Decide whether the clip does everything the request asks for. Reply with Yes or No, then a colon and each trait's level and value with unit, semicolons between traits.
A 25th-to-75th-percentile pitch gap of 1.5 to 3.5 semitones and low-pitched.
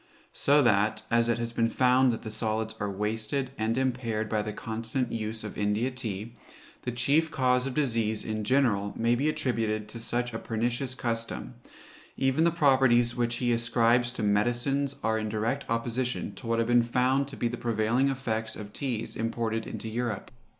Yes: narrow, 2.4 semitones; low, 115 Hz